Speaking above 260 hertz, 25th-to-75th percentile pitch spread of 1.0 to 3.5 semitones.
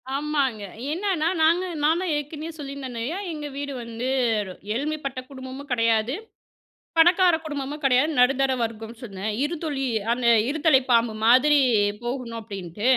No: very high, 275 Hz; average, 4.2 semitones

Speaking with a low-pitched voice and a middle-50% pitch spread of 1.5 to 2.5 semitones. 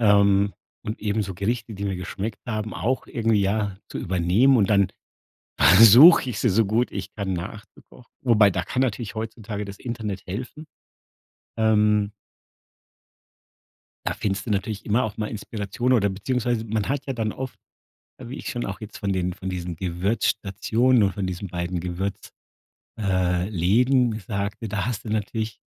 No: low, 105 Hz; average, 2.9 semitones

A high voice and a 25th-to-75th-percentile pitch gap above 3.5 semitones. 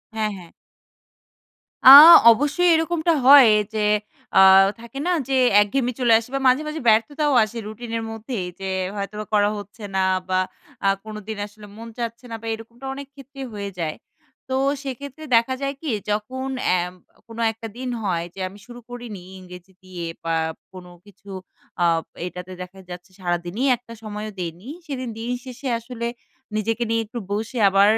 Yes: high, 225 Hz; average, 4.3 semitones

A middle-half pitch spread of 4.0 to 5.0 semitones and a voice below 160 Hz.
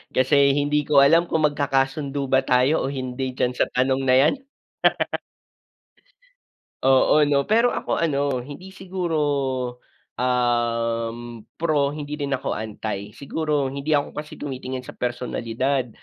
No: average, 2.7 semitones; low, 135 Hz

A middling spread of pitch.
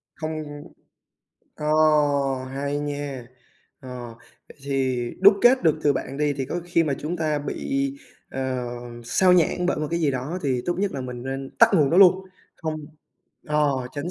Yes: average, 4.4 semitones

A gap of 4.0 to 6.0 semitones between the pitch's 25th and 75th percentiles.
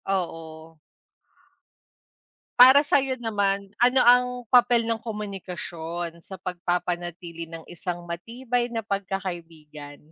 Yes: average, 5.2 semitones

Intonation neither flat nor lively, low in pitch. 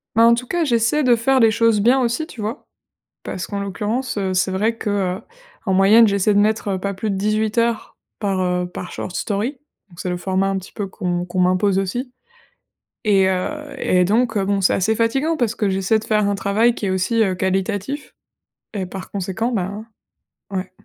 No: average, 3.3 semitones; high, 205 Hz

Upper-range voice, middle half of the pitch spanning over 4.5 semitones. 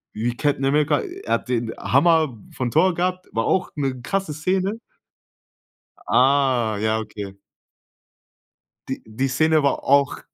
No: medium, 140 Hz; average, 4.9 semitones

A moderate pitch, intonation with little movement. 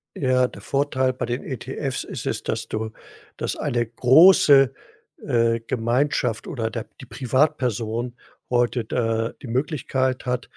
No: low, 125 Hz; narrow, 2.2 semitones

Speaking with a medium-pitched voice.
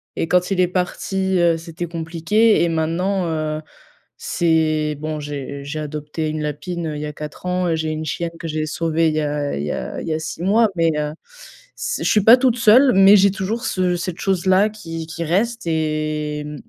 Yes: medium, 165 Hz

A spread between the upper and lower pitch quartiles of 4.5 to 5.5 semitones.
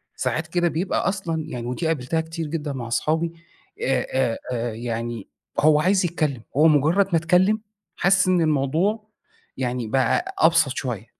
Yes: average, 5.2 semitones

